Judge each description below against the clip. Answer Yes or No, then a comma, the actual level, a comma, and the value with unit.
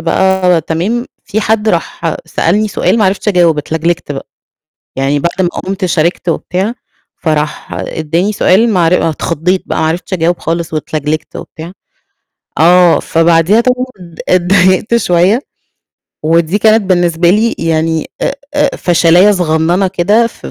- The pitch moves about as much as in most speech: Yes, average, 3.3 semitones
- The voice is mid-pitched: Yes, medium, 175 Hz